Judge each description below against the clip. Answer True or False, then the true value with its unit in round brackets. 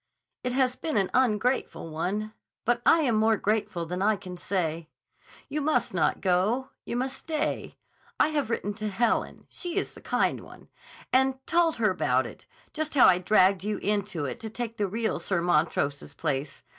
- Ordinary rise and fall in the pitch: False (5.9 semitones)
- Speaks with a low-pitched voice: False (215 Hz)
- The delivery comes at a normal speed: True (175 wpm)